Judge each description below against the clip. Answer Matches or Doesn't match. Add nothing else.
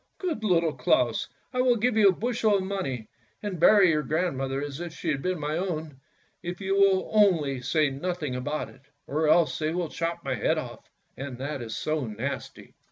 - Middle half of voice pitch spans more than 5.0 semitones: Matches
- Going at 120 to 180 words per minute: Doesn't match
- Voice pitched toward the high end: Doesn't match